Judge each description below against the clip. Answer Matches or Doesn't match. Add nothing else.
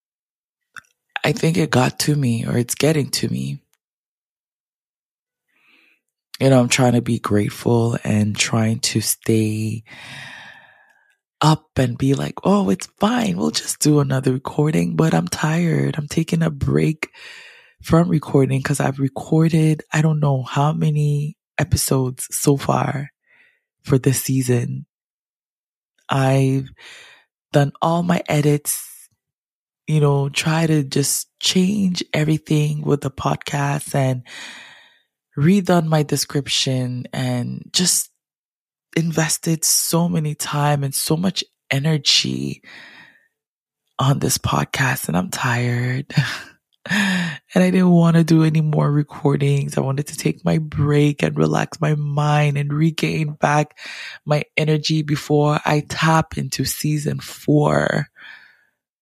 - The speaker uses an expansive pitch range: Doesn't match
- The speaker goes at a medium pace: Doesn't match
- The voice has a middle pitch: Matches